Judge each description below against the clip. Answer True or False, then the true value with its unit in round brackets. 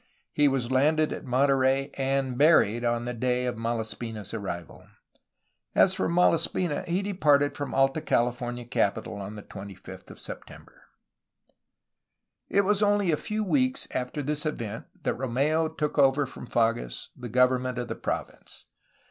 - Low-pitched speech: True (130 Hz)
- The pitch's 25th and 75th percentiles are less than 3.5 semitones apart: False (4.5 semitones)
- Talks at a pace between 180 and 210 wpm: False (155 wpm)